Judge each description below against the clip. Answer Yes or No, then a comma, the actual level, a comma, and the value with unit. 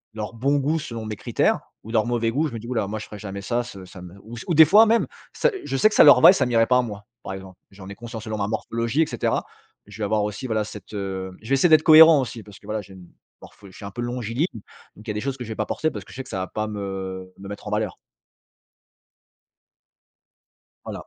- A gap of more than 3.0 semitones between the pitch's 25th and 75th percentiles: Yes, average, 4.1 semitones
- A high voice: No, low, 110 Hz